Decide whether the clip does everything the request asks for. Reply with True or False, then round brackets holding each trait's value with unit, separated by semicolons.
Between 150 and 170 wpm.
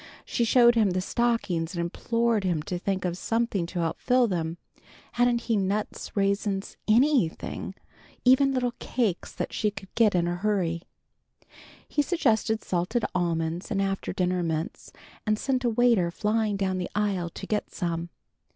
True (160 wpm)